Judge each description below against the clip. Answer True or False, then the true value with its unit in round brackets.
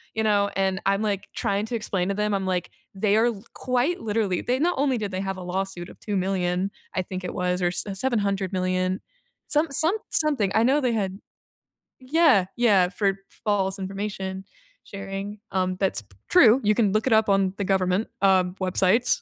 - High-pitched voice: True (195 Hz)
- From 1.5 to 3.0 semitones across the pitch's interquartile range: True (2.7 semitones)